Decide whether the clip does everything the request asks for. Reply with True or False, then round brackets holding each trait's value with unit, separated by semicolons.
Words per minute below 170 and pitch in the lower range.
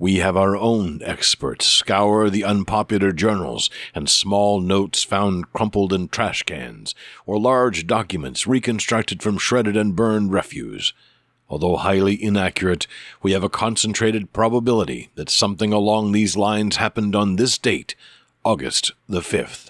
True (140 wpm; 105 Hz)